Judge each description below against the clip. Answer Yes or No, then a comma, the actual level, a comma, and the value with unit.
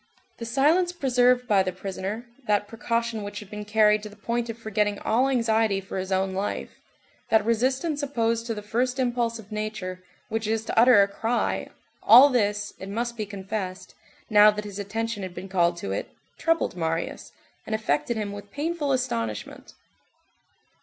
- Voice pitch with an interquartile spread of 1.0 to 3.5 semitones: Yes, average, 2.9 semitones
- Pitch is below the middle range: No, high, 215 Hz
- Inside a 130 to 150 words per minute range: No, average, 175 wpm